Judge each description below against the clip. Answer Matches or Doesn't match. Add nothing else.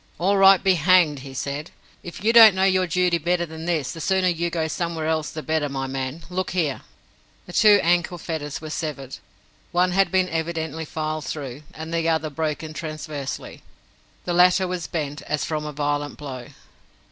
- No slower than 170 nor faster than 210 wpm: Matches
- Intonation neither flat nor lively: Matches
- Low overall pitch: Doesn't match